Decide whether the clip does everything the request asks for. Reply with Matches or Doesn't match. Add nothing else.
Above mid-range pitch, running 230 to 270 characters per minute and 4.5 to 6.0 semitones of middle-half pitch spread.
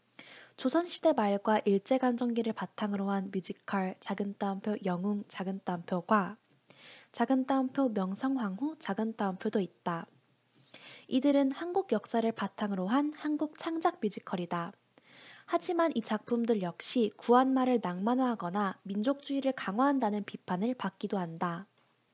Doesn't match